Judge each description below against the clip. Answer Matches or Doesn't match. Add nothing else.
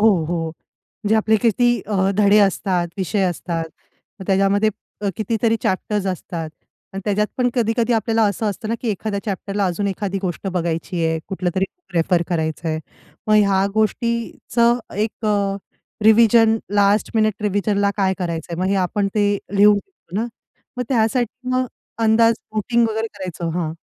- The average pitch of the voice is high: Matches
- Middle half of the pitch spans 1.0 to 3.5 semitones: Matches